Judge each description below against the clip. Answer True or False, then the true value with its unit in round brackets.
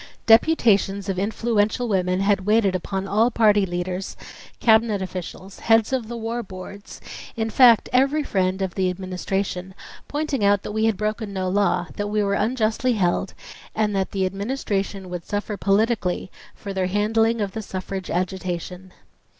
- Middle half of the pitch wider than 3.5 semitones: False (2.9 semitones)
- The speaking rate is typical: True (160 wpm)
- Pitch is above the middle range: True (200 Hz)